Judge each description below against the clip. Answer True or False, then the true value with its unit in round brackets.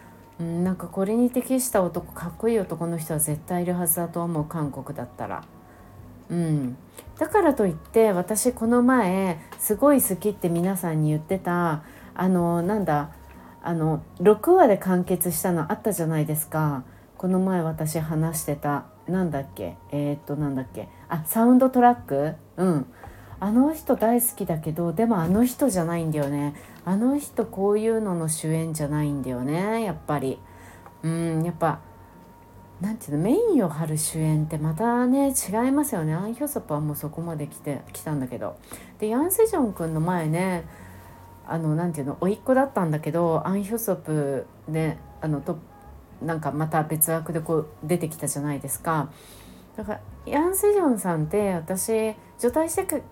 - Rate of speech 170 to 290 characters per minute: False (335 characters per minute)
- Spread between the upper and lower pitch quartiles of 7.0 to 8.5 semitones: False (5.9 semitones)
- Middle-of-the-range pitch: True (170 Hz)